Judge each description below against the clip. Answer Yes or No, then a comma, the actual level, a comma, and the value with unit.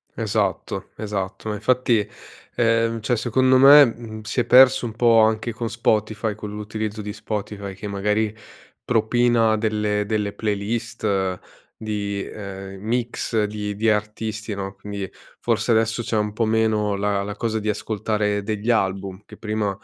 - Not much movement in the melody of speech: Yes, narrow, 1.7 semitones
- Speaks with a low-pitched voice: Yes, low, 110 Hz